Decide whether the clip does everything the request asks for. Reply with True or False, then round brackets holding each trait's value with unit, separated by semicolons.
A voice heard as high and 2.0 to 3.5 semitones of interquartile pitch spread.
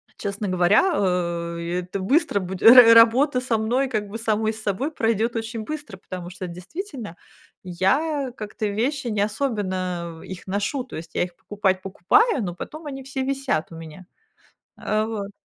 False (215 Hz; 5.6 semitones)